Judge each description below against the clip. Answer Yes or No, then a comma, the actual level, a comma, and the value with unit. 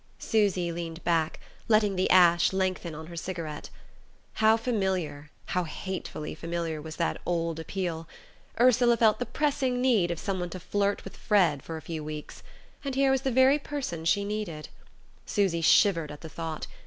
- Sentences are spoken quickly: No, average, 165 wpm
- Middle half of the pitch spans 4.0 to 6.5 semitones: Yes, average, 4.7 semitones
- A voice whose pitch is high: No, medium, 180 Hz